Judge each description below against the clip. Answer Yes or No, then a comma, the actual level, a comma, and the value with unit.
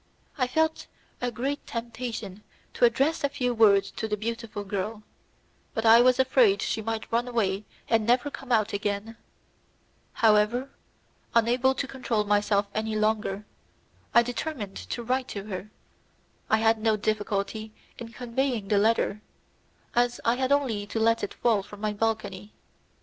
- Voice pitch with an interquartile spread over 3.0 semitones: No, average, 2.7 semitones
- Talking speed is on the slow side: No, average, 155 wpm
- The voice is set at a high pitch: Yes, high, 225 Hz